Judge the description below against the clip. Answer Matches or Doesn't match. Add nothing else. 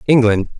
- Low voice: Matches